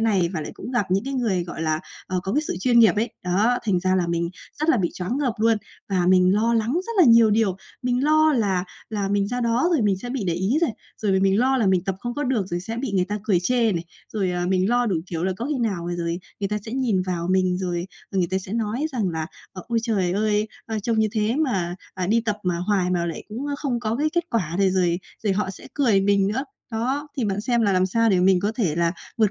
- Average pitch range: Yes, average, 4.3 semitones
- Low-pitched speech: No, high, 205 Hz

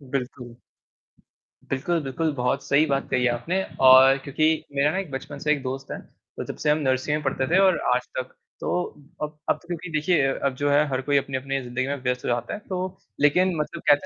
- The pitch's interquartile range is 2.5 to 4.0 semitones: Yes, average, 2.8 semitones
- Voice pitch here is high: No, medium, 140 Hz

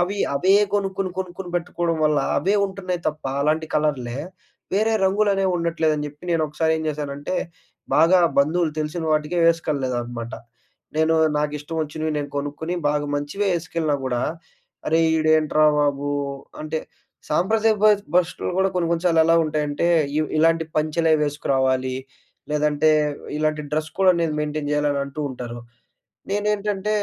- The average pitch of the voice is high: No, medium, 155 Hz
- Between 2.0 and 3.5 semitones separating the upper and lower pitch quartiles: Yes, average, 3.0 semitones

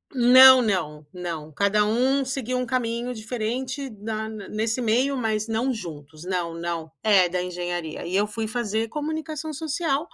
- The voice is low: No, high, 220 Hz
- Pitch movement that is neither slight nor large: No, wide, 5.9 semitones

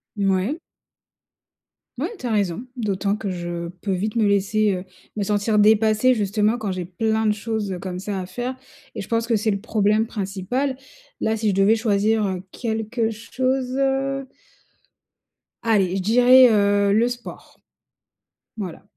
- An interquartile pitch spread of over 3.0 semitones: No, average, 2.7 semitones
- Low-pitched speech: No, high, 215 Hz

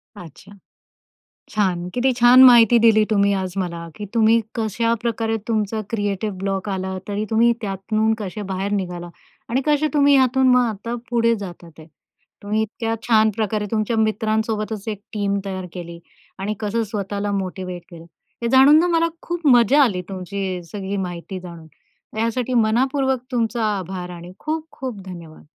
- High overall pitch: Yes, high, 215 Hz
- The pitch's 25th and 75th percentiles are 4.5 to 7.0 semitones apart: No, average, 3.6 semitones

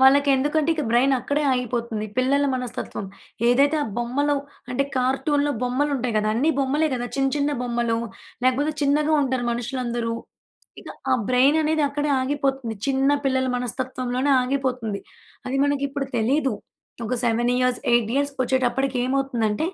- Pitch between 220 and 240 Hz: No, very high, 260 Hz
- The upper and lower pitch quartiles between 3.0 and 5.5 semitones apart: No, narrow, 2.5 semitones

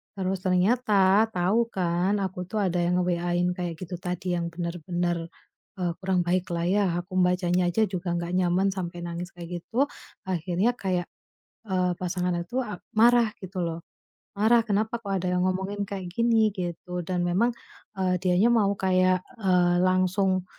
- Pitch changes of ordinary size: No, narrow, 1.9 semitones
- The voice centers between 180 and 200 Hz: Yes, medium, 185 Hz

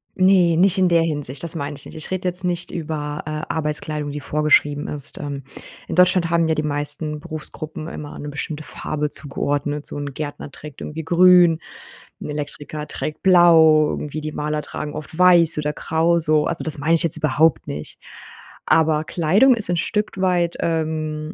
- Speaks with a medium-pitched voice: Yes, medium, 155 Hz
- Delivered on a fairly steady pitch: Yes, narrow, 2.3 semitones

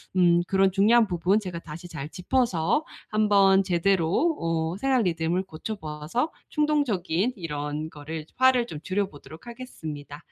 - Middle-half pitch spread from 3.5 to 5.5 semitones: Yes, average, 5.1 semitones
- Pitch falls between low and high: Yes, medium, 180 Hz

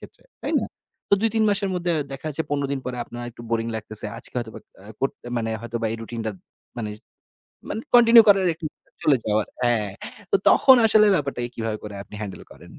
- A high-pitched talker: No, low, 120 Hz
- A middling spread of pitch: No, wide, 8.1 semitones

